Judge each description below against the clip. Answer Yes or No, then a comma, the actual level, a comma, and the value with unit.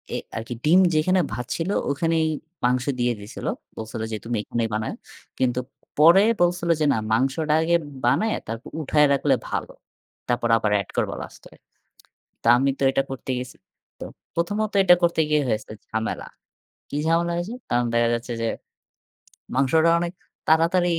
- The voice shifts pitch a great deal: Yes, wide, 6.1 semitones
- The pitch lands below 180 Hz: Yes, medium, 140 Hz